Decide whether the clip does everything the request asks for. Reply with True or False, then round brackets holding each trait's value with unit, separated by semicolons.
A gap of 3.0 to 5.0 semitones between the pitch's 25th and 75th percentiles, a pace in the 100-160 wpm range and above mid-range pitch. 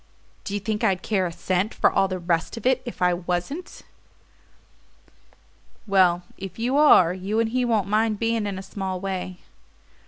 False (3.5 semitones; 180 wpm; 195 Hz)